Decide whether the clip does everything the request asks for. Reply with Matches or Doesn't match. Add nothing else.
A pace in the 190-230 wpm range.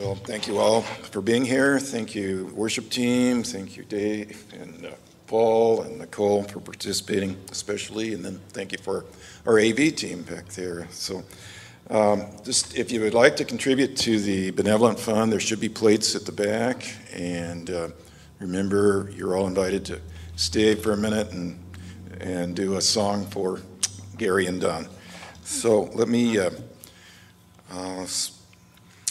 Doesn't match